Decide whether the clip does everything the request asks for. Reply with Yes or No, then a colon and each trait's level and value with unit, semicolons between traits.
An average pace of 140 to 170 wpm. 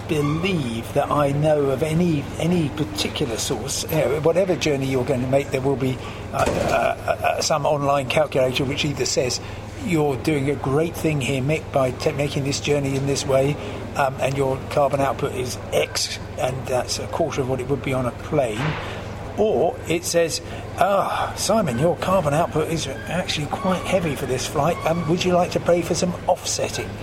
No: average, 200 wpm